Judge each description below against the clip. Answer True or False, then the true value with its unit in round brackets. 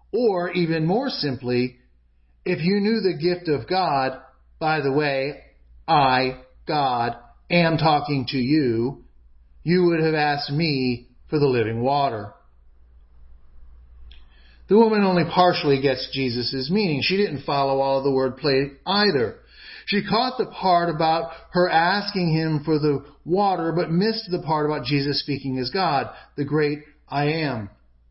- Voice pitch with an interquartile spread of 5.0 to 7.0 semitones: True (5.4 semitones)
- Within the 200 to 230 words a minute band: False (145 wpm)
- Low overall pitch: False (145 Hz)